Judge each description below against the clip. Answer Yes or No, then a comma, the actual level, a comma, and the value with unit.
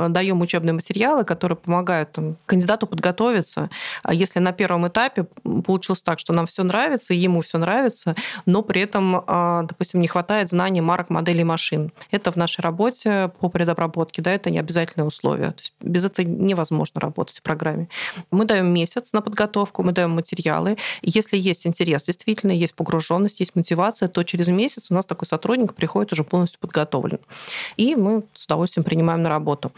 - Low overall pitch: No, medium, 180 Hz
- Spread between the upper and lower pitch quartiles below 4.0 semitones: Yes, average, 3.1 semitones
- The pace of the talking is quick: Yes, fast, 165 wpm